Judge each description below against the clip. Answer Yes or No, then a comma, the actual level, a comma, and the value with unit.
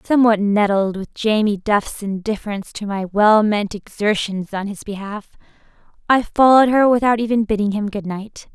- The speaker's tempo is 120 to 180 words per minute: Yes, average, 160 wpm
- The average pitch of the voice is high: Yes, high, 210 Hz